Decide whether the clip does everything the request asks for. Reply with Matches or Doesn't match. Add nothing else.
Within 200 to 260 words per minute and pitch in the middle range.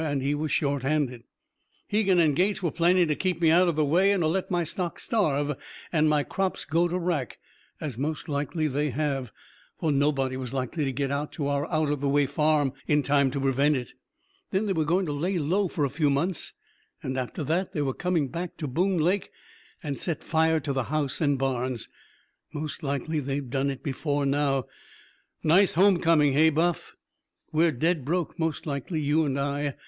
Matches